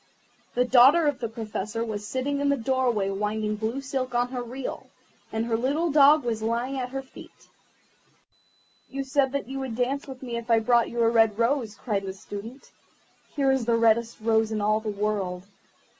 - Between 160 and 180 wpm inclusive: No, average, 195 wpm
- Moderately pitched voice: No, high, 235 Hz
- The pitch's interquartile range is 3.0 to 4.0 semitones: Yes, average, 3.4 semitones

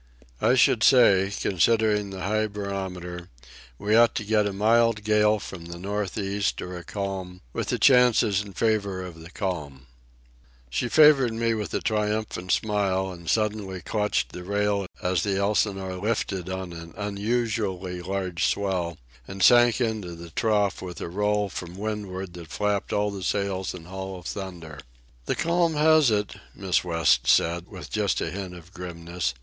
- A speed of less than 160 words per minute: No, average, 165 wpm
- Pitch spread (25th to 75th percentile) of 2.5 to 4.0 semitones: Yes, average, 2.9 semitones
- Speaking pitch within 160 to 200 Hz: No, low, 100 Hz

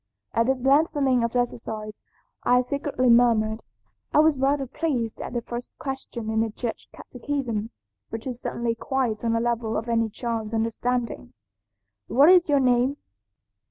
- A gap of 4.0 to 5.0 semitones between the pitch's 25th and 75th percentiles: No, average, 2.9 semitones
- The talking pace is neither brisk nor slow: Yes, average, 155 wpm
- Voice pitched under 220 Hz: No, high, 240 Hz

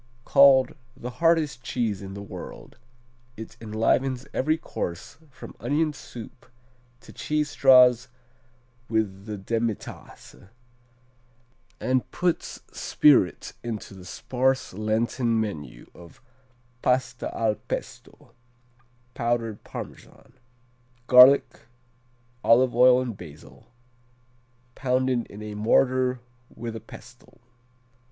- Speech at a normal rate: No, slow, 100 wpm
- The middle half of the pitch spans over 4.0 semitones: No, average, 3.3 semitones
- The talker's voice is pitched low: Yes, low, 120 Hz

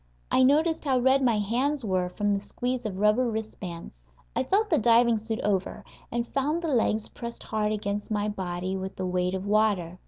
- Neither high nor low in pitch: No, high, 215 Hz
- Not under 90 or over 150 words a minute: No, average, 200 wpm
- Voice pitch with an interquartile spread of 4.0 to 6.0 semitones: Yes, average, 4.5 semitones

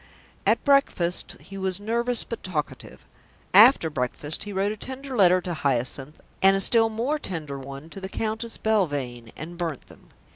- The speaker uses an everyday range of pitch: No, wide, 6.8 semitones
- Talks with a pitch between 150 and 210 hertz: Yes, high, 190 Hz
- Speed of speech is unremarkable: Yes, average, 170 wpm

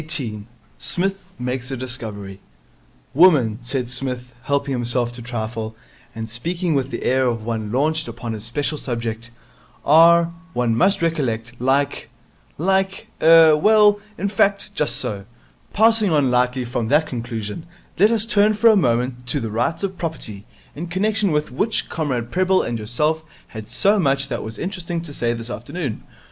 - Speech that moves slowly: No, average, 160 wpm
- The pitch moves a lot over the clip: Yes, wide, 6.4 semitones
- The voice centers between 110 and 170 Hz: Yes, low, 135 Hz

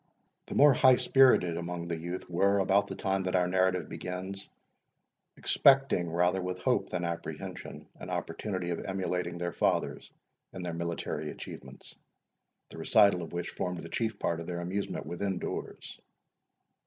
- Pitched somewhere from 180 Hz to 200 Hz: No, very low, 90 Hz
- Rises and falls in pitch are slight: Yes, narrow, 2.1 semitones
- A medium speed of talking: Yes, average, 155 wpm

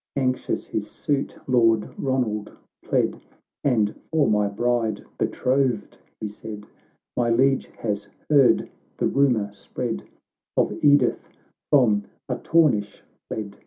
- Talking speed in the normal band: No, slow, 125 wpm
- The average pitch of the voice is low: Yes, low, 120 Hz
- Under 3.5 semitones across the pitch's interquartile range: No, average, 4.3 semitones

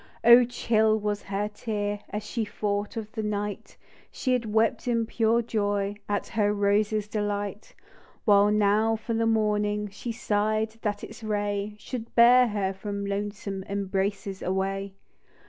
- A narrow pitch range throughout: Yes, narrow, 1.4 semitones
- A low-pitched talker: No, high, 210 Hz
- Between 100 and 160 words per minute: Yes, average, 150 wpm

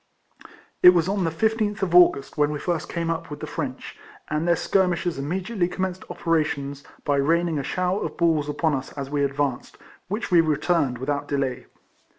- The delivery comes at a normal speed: Yes, average, 185 wpm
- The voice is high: No, medium, 160 Hz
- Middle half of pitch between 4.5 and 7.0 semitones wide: No, average, 3.8 semitones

